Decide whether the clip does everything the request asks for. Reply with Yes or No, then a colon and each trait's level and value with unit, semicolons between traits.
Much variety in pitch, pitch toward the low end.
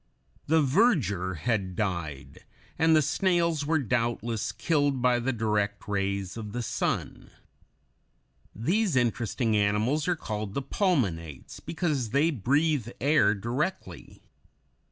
Yes: wide, 6.9 semitones; low, 120 Hz